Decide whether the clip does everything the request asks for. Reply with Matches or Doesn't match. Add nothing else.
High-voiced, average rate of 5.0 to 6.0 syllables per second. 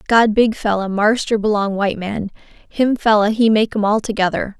Matches